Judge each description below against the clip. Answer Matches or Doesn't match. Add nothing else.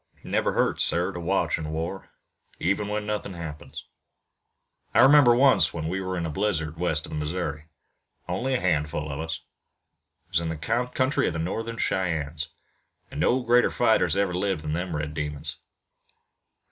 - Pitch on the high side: Doesn't match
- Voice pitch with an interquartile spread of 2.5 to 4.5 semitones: Doesn't match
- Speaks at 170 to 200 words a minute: Matches